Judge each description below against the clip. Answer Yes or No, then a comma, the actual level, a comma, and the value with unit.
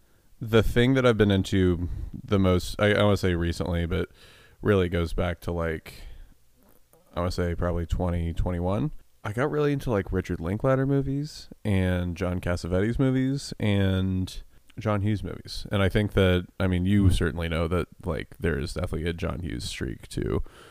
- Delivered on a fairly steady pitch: No, average, 3.3 semitones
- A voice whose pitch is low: Yes, very low, 95 Hz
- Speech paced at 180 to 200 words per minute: Yes, average, 185 wpm